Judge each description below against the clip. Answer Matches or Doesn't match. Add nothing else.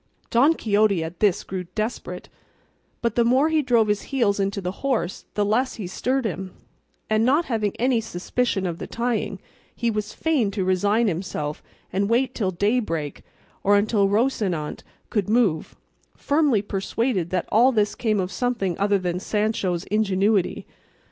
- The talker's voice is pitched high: Matches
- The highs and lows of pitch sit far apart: Doesn't match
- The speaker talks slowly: Doesn't match